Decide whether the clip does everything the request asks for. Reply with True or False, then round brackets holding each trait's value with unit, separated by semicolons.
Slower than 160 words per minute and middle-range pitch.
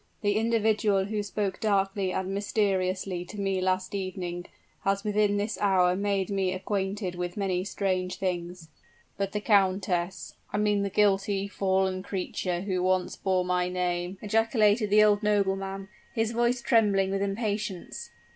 False (145 wpm; 195 Hz)